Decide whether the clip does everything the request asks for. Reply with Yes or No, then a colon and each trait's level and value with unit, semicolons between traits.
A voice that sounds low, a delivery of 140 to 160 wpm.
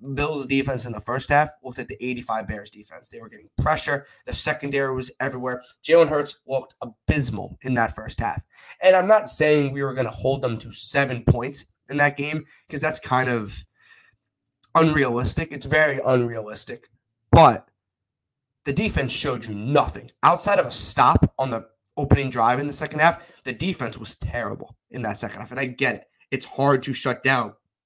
No: low, 130 Hz; average, 185 wpm